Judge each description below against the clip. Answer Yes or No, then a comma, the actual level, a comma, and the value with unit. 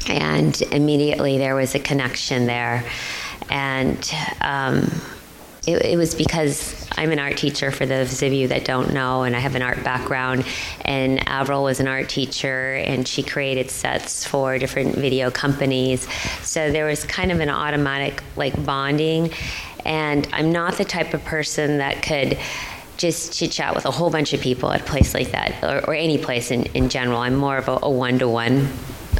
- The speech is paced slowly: No, average, 185 wpm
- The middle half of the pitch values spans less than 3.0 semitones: Yes, narrow, 2.4 semitones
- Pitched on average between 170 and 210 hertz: No, low, 135 Hz